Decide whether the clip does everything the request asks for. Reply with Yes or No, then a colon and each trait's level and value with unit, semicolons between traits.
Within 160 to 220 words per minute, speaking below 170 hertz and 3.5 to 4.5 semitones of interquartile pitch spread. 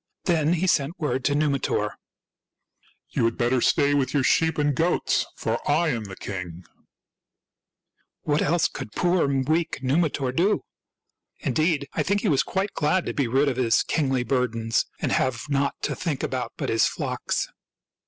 Yes: average, 180 wpm; medium, 140 Hz; average, 4.2 semitones